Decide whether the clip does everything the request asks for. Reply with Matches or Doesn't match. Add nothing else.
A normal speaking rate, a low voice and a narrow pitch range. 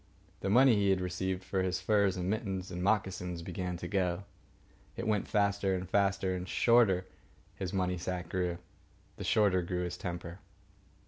Matches